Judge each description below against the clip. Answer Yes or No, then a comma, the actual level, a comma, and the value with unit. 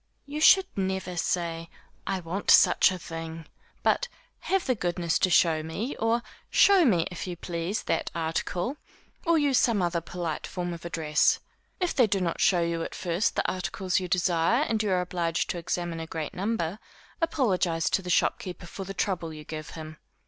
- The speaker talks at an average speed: Yes, average, 185 wpm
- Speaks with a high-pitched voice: No, medium, 180 Hz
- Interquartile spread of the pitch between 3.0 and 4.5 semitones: Yes, average, 3.6 semitones